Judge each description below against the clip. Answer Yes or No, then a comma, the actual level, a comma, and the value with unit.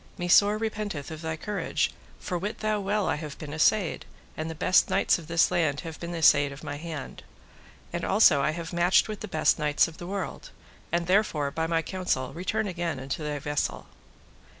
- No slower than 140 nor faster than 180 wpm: No, average, 200 wpm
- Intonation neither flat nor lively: Yes, average, 4.0 semitones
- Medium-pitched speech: Yes, medium, 170 Hz